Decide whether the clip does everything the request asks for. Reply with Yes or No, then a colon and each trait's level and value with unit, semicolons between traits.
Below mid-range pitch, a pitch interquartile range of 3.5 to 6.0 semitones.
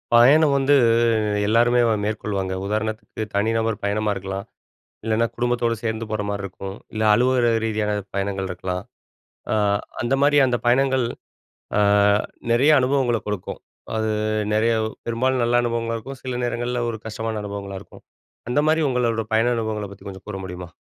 No: low, 115 Hz; average, 2.8 semitones